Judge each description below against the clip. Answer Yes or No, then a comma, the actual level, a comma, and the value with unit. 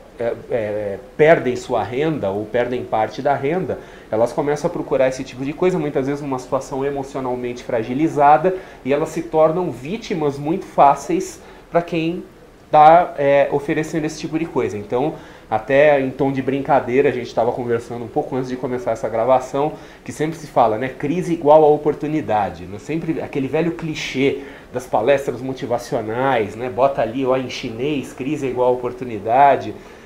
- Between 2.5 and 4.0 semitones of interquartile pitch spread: Yes, average, 3.6 semitones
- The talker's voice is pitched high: No, medium, 140 Hz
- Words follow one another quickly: No, average, 170 wpm